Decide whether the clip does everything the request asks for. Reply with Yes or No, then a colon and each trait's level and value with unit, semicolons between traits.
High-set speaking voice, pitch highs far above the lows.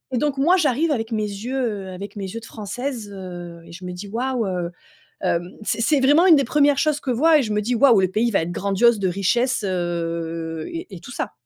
Yes: high, 220 Hz; wide, 6.3 semitones